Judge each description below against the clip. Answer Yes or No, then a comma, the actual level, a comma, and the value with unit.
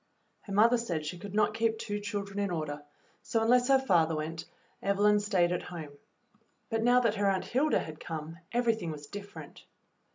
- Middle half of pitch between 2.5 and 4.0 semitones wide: No, average, 5.1 semitones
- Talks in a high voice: Yes, high, 205 Hz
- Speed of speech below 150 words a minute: No, average, 185 wpm